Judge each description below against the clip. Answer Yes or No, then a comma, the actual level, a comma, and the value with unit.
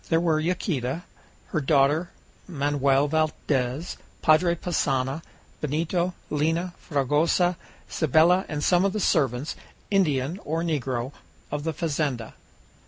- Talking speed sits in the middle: No, slow, 110 wpm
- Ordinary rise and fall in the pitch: Yes, average, 3.6 semitones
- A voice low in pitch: No, medium, 155 Hz